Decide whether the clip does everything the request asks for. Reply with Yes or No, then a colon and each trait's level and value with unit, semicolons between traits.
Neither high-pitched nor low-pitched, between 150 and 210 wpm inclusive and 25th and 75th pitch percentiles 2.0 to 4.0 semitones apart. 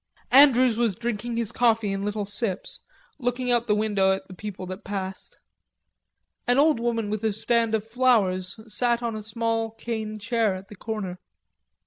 No: high, 220 Hz; average, 175 wpm; narrow, 2.5 semitones